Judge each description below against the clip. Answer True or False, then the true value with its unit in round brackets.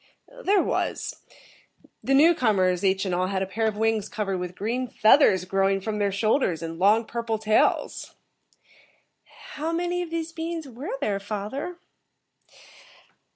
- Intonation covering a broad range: True (6.6 semitones)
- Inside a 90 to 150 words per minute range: True (145 wpm)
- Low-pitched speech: False (215 Hz)